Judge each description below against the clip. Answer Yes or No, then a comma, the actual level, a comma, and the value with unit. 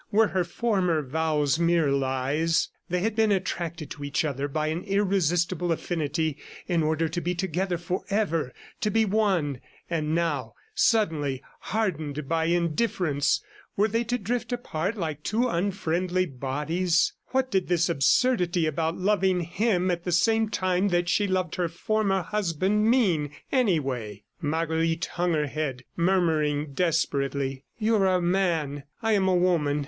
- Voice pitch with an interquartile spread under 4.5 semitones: Yes, average, 4.0 semitones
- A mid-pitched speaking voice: Yes, medium, 175 Hz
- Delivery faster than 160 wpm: No, average, 150 wpm